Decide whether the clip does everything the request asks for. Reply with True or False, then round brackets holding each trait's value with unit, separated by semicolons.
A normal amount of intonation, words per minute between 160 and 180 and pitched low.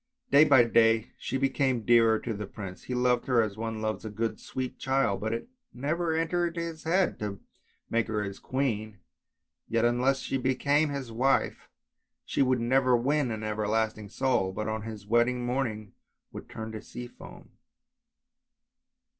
True (3.5 semitones; 165 wpm; 120 Hz)